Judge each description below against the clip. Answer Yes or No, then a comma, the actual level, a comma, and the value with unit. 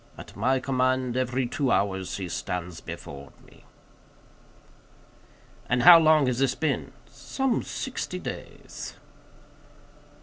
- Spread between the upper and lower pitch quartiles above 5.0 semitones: Yes, wide, 5.6 semitones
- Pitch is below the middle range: Yes, low, 130 Hz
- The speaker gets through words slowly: Yes, slow, 110 wpm